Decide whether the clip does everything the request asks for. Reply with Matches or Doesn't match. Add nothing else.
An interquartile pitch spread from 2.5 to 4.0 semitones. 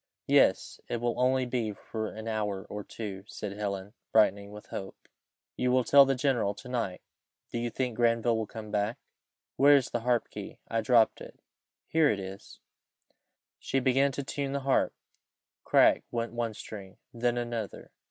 Matches